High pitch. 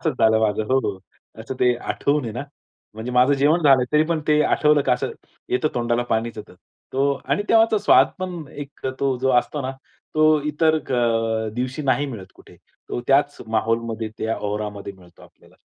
No: low, 130 Hz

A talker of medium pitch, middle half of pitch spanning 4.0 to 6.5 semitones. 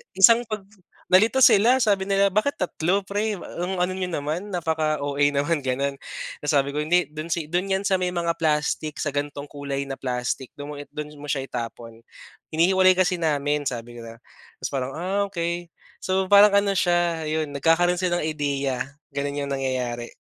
Yes: medium, 160 Hz; average, 4.7 semitones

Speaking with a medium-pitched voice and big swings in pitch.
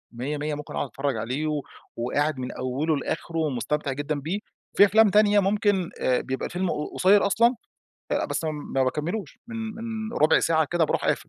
Yes: medium, 155 Hz; wide, 6.0 semitones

